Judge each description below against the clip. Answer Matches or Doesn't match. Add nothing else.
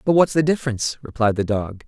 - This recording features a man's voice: Matches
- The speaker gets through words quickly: Matches